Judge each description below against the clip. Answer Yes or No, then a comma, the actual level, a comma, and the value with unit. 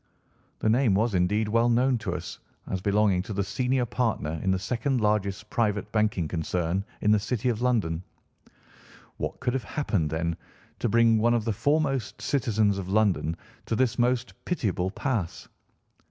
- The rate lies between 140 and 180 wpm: Yes, average, 170 wpm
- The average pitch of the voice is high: No, low, 105 Hz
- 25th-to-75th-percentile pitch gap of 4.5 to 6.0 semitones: No, average, 4.0 semitones